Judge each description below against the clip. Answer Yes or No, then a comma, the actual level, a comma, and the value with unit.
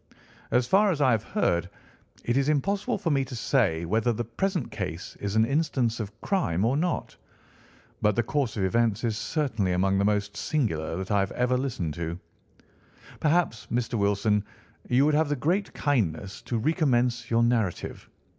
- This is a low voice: Yes, low, 120 Hz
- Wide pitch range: Yes, wide, 6.1 semitones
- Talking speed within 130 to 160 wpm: No, average, 175 wpm